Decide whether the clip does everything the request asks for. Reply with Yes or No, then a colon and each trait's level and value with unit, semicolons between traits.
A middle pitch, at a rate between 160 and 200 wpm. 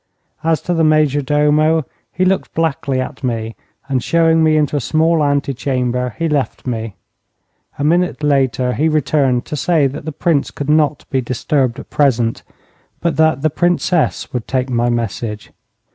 Yes: medium, 145 Hz; average, 170 wpm